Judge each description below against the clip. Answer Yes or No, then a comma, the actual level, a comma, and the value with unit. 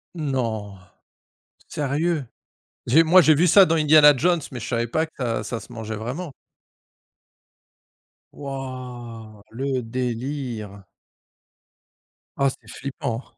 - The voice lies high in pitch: No, low, 130 Hz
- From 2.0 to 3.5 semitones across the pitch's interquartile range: No, average, 4.6 semitones